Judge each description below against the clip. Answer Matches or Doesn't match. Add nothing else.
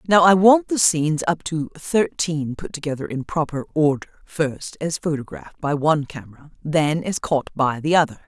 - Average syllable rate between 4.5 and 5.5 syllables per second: Matches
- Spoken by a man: Doesn't match